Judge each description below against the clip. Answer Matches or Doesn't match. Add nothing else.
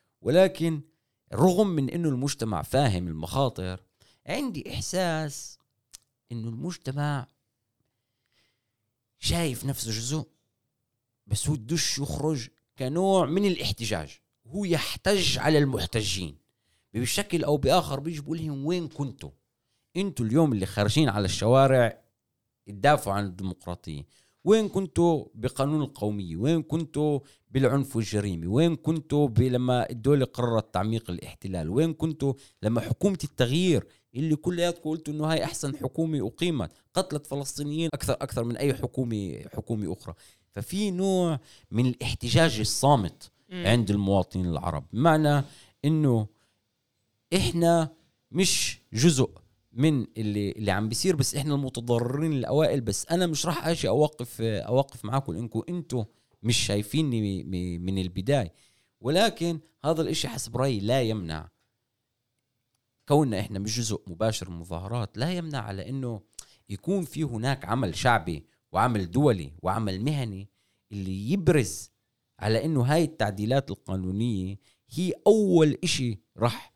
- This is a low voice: Matches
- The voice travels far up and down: Matches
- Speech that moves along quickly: Doesn't match